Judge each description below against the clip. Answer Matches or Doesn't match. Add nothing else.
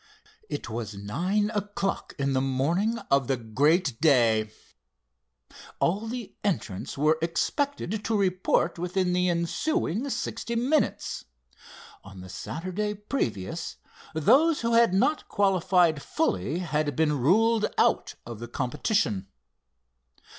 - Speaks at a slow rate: Matches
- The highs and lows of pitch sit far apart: Matches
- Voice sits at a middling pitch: Matches